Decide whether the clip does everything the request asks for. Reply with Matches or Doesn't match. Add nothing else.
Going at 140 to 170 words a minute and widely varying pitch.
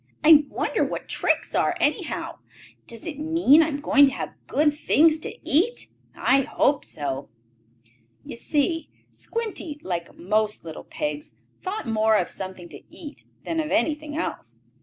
Matches